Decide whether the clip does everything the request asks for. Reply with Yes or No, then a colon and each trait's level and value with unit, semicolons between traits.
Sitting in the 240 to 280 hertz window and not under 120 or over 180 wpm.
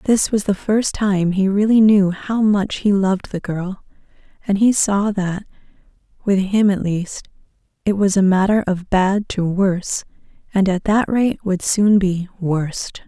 No: high, 195 Hz; average, 170 wpm